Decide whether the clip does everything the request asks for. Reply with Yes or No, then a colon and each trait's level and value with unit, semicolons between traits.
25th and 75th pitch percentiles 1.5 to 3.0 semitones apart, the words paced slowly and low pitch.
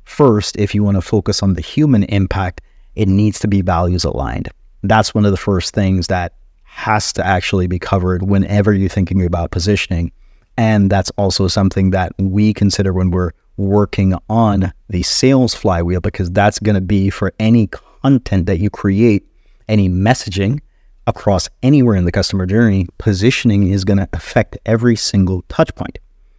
No: narrow, 2.6 semitones; average, 170 wpm; low, 100 Hz